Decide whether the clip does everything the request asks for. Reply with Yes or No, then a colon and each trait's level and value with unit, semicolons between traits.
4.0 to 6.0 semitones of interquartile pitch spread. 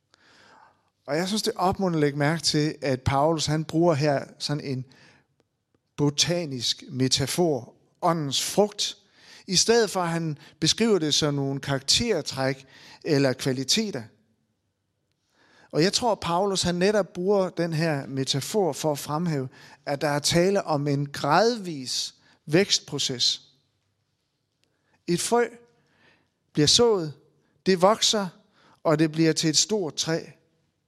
Yes: average, 4.6 semitones